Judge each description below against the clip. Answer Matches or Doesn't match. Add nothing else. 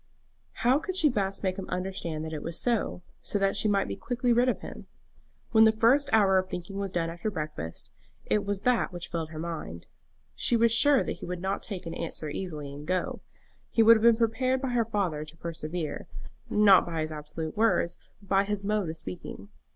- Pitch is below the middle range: Doesn't match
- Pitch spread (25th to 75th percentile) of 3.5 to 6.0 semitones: Matches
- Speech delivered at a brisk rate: Matches